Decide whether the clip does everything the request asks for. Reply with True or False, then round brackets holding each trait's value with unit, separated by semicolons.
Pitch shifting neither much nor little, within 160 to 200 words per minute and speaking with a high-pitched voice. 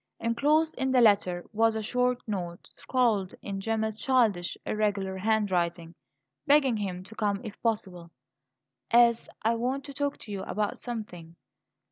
False (4.0 semitones; 145 wpm; 215 Hz)